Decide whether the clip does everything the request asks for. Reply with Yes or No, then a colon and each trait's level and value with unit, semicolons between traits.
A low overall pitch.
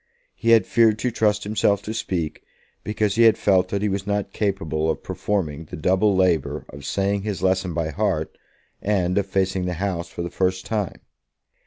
Yes: very low, 95 Hz